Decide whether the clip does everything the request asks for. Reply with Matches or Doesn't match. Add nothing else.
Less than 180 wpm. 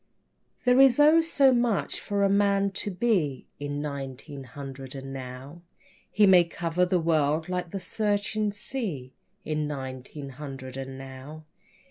Matches